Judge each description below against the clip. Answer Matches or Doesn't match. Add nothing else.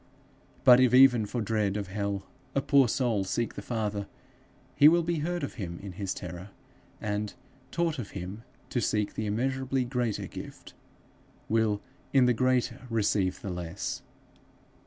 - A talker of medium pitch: Doesn't match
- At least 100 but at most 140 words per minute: Doesn't match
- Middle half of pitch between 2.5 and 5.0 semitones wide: Matches